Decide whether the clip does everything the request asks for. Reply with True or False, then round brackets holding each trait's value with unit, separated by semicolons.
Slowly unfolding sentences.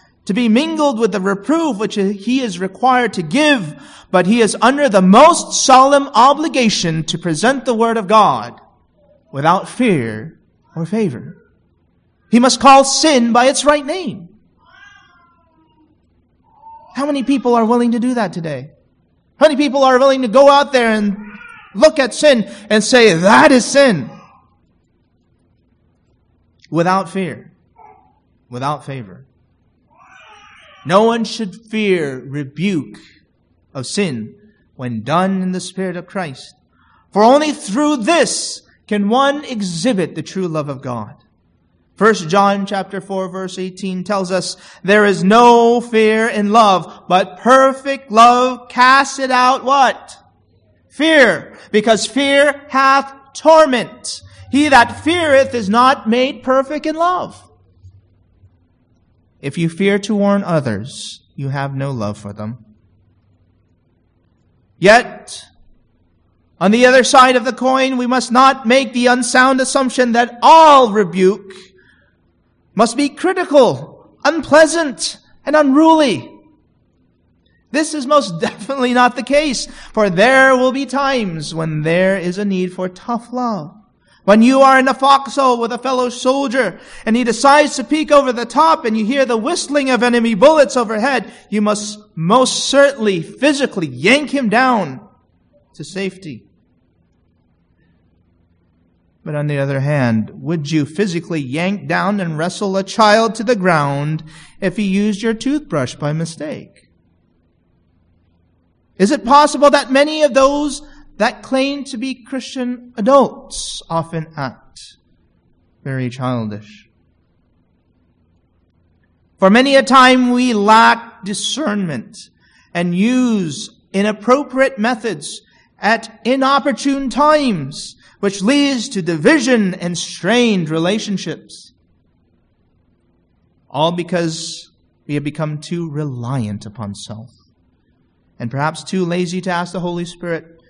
True (130 wpm)